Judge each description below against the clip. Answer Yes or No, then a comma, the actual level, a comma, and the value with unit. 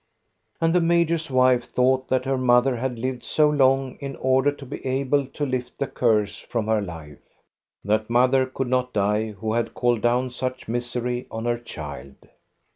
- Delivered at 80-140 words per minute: No, average, 180 wpm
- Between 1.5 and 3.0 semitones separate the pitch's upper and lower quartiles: Yes, narrow, 2.4 semitones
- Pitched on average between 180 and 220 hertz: No, low, 125 Hz